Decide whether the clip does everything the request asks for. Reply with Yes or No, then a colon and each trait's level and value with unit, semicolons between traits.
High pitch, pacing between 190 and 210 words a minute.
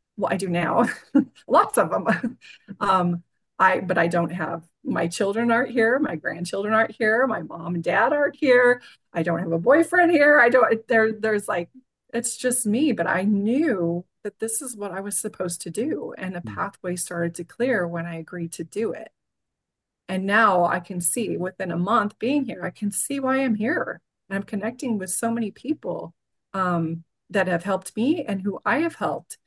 Yes: high, 205 Hz; average, 200 wpm